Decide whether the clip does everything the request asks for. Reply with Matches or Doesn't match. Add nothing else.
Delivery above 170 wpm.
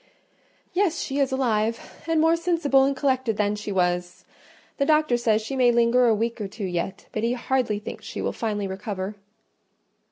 Matches